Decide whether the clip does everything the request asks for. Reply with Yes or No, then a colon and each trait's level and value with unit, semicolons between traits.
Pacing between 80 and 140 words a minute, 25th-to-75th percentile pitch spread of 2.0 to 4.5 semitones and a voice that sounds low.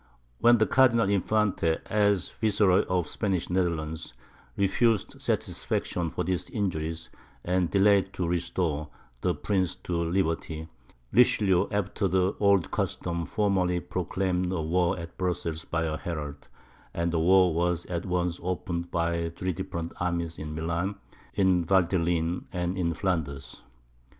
Yes: slow, 135 wpm; narrow, 2.4 semitones; very low, 90 Hz